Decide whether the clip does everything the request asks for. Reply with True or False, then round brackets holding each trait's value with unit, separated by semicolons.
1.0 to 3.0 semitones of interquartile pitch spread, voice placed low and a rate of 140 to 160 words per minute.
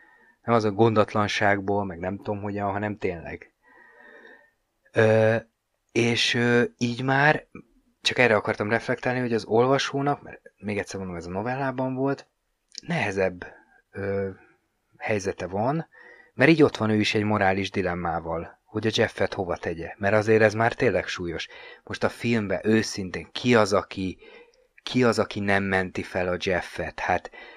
False (3.7 semitones; 110 Hz; 150 wpm)